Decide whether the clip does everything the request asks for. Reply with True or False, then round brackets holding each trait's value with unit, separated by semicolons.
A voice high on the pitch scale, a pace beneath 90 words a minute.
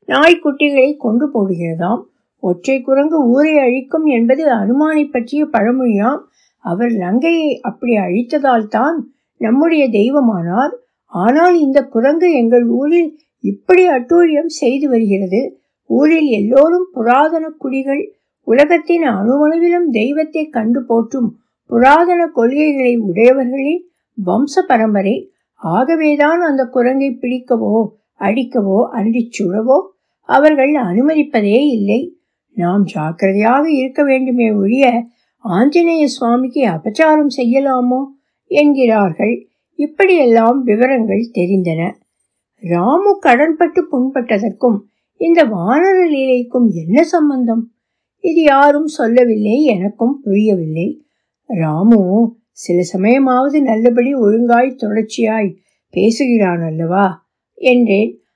True (250 Hz; 80 wpm)